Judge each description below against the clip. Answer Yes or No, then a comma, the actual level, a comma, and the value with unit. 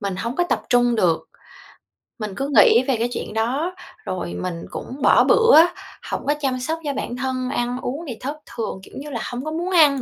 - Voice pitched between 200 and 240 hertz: No, very high, 255 Hz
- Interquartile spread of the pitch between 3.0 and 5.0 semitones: Yes, average, 4.2 semitones